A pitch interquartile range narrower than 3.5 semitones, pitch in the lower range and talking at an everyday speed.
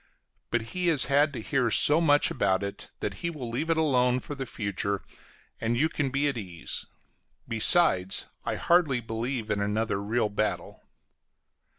No: wide, 5.4 semitones; low, 125 Hz; average, 170 wpm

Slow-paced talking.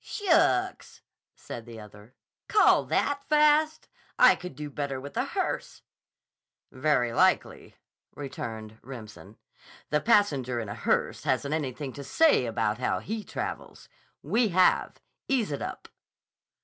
Yes: slow, 130 wpm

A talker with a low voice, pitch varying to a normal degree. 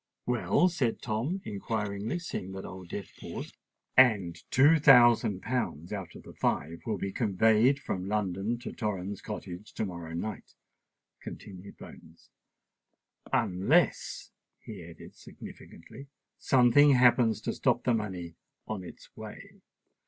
Yes: low, 105 Hz; average, 4.8 semitones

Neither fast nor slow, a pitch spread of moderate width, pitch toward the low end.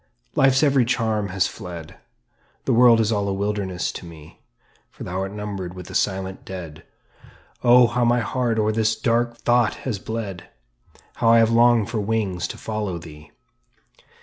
Yes: average, 170 wpm; average, 3.8 semitones; low, 105 Hz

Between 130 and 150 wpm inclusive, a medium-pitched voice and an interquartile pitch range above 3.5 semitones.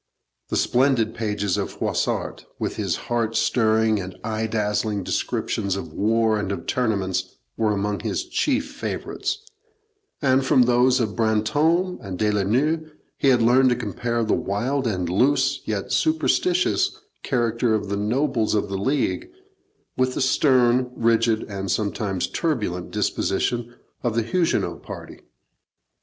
No: average, 140 wpm; low, 115 Hz; average, 3.9 semitones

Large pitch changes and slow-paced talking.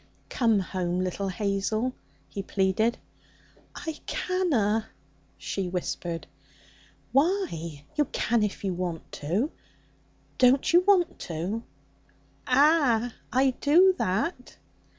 Yes: wide, 7.5 semitones; slow, 100 wpm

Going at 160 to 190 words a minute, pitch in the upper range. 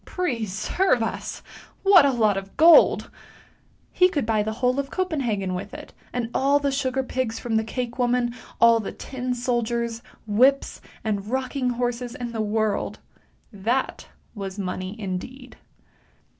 No: average, 150 wpm; high, 240 Hz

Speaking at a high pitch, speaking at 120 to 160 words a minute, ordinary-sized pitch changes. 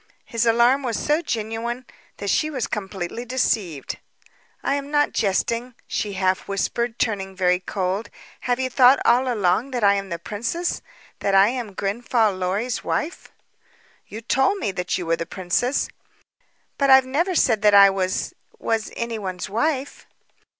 Yes: high, 225 Hz; average, 155 wpm; average, 4.7 semitones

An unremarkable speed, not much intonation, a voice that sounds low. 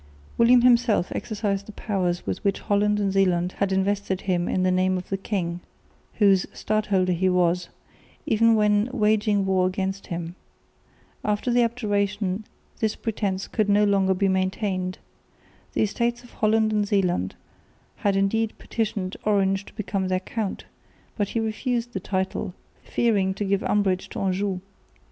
No: average, 155 wpm; narrow, 2.3 semitones; high, 200 Hz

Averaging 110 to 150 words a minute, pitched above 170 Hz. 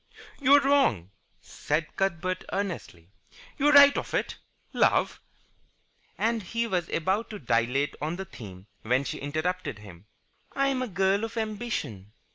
Yes: average, 145 wpm; medium, 185 Hz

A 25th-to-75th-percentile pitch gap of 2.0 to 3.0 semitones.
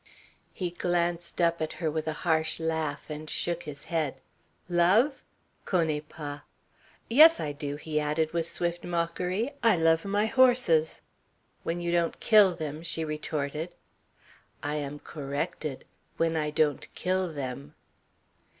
Yes: narrow, 2.5 semitones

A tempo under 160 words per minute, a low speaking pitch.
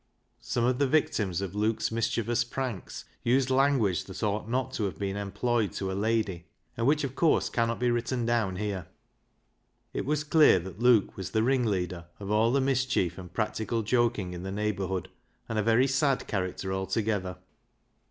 No: average, 175 wpm; low, 110 Hz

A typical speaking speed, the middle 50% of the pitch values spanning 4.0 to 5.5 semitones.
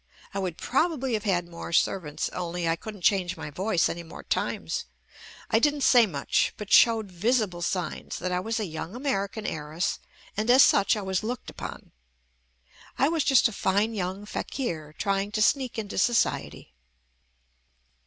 Yes: average, 165 wpm; average, 4.5 semitones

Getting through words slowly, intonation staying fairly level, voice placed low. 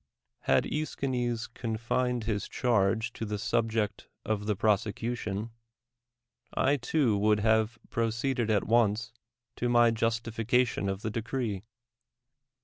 Yes: slow, 125 wpm; narrow, 2.1 semitones; low, 115 Hz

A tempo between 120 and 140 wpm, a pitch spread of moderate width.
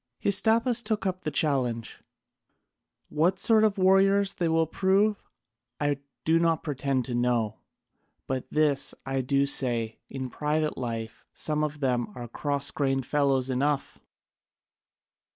No: slow, 135 wpm; wide, 5.9 semitones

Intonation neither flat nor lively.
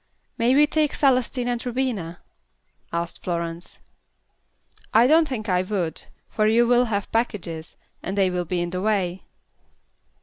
No: wide, 5.7 semitones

